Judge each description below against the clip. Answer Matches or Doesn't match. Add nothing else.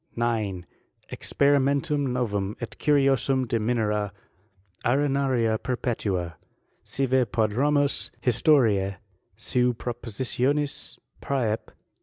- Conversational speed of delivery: Doesn't match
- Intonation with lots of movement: Doesn't match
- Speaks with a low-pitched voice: Matches